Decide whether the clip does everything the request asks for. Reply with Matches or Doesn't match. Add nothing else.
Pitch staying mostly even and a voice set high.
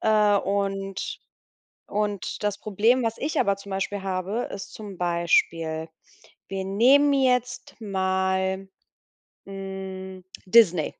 Matches